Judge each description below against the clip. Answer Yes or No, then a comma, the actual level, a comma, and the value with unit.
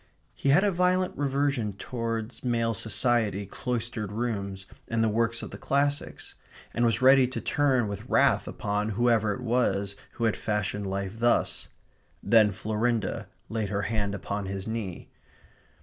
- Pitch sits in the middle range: No, low, 115 Hz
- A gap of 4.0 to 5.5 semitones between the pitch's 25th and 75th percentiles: No, average, 3.1 semitones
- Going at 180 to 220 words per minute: No, average, 150 wpm